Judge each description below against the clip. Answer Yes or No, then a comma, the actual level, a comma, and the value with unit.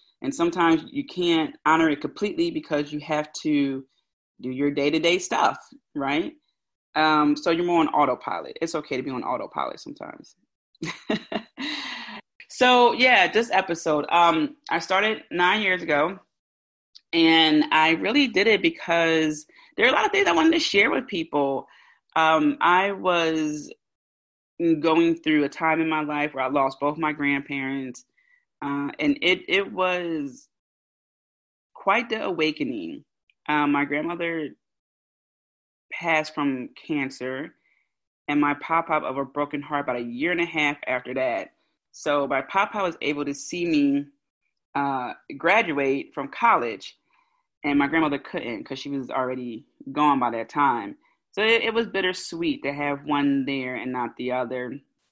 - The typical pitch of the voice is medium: Yes, medium, 155 Hz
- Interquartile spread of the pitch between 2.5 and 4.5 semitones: No, average, 5.0 semitones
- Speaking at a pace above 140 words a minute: Yes, average, 155 wpm